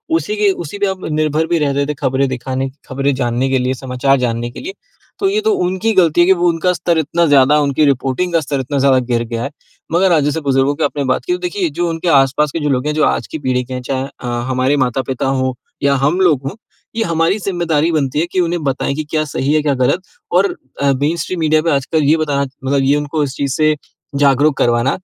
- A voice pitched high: No, medium, 145 Hz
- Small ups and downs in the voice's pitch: No, average, 3.9 semitones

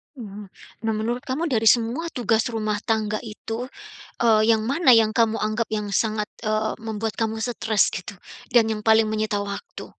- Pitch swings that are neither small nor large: No, narrow, 1.3 semitones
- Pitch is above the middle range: Yes, high, 220 Hz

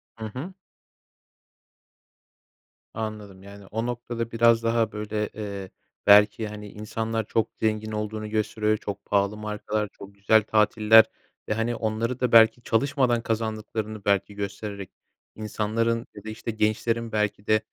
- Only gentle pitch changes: Yes, narrow, 1.4 semitones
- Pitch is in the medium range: No, low, 110 Hz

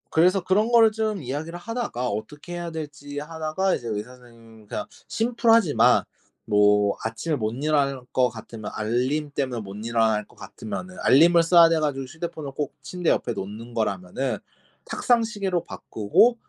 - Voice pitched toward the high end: No, medium, 145 Hz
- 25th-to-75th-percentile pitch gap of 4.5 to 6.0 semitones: No, wide, 7.4 semitones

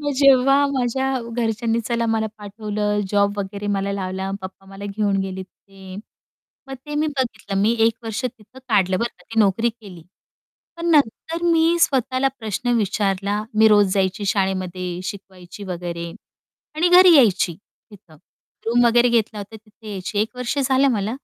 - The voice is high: Yes, high, 215 Hz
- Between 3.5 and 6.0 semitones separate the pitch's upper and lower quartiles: Yes, average, 4.0 semitones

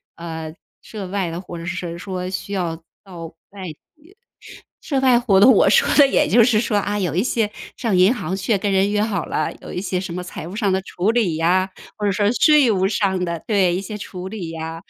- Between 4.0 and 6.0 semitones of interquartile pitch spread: No, average, 2.9 semitones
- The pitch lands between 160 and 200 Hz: Yes, high, 190 Hz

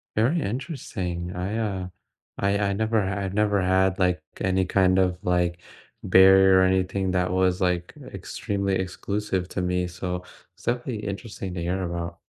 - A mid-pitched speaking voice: No, very low, 95 Hz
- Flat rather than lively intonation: Yes, narrow, 1.7 semitones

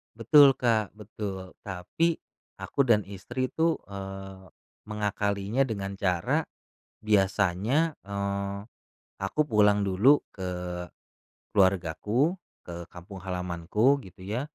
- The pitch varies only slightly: No, average, 3.5 semitones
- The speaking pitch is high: No, low, 100 Hz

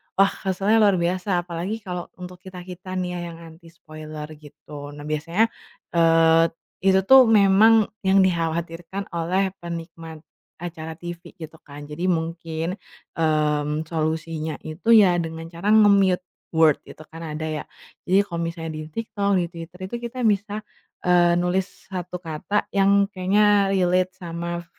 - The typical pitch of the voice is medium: Yes, medium, 175 Hz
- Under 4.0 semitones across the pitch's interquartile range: Yes, average, 2.9 semitones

